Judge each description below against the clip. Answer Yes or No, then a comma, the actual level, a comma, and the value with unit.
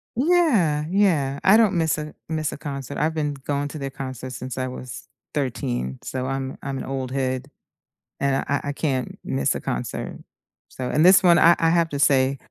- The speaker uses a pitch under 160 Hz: Yes, medium, 140 Hz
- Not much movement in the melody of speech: No, average, 3.6 semitones